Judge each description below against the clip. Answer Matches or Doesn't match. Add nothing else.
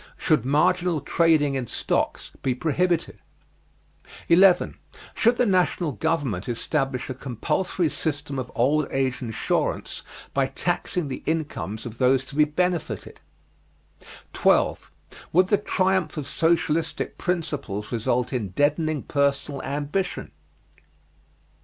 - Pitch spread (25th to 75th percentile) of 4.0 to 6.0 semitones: Matches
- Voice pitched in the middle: Matches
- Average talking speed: Doesn't match